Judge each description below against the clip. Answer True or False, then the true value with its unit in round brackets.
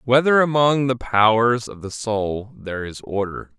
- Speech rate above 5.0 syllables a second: False (4.3 syllables/s)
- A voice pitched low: True (115 Hz)